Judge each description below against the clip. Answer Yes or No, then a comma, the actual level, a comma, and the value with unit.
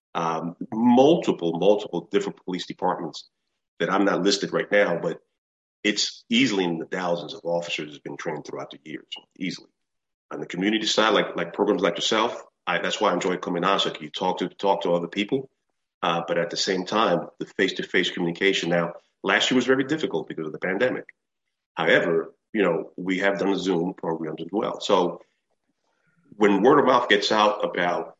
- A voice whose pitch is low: Yes, very low, 90 Hz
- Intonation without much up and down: No, average, 3.4 semitones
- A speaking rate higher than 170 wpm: Yes, average, 190 wpm